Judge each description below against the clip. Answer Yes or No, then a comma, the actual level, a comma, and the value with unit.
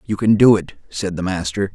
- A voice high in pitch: No, very low, 95 Hz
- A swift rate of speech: Yes, fast, 240 wpm